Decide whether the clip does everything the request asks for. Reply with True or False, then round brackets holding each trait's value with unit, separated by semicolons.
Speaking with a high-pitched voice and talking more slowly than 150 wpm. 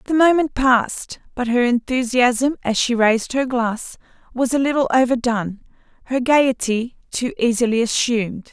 True (245 Hz; 140 wpm)